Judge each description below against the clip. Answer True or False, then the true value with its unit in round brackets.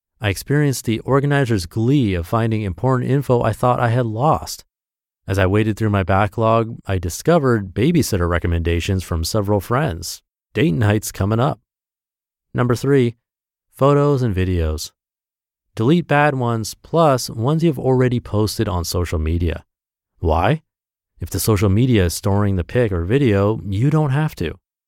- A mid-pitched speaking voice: False (110 Hz)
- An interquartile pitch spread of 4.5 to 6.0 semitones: True (5.2 semitones)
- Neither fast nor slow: True (150 wpm)